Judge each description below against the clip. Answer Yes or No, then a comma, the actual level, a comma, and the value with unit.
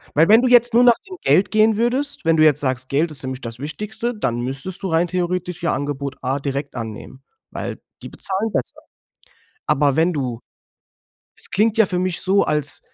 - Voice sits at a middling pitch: Yes, medium, 165 Hz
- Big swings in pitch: Yes, wide, 7.4 semitones